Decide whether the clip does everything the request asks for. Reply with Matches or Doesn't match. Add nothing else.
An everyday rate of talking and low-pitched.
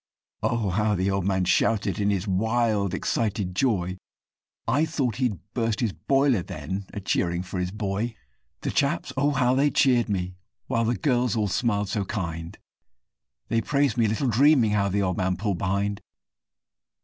Matches